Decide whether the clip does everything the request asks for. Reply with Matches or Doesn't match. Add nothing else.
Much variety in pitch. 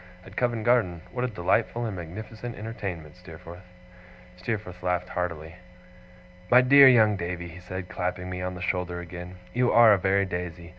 Doesn't match